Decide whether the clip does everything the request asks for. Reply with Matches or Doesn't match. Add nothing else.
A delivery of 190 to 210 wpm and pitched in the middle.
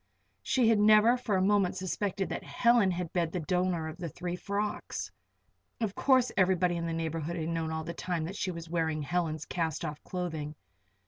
Matches